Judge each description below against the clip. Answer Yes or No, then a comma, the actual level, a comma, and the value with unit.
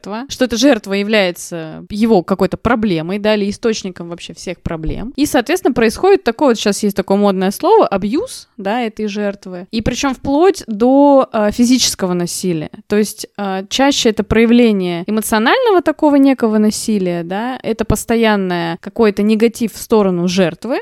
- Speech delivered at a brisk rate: No, average, 150 wpm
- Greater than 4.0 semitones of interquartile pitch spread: Yes, average, 4.4 semitones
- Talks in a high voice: Yes, high, 215 Hz